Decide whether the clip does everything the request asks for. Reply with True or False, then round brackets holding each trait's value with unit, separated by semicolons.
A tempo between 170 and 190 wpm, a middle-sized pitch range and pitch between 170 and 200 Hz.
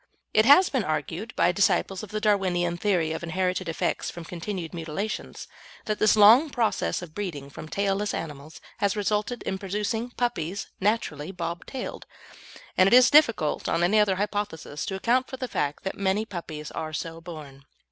True (175 wpm; 4.5 semitones; 190 Hz)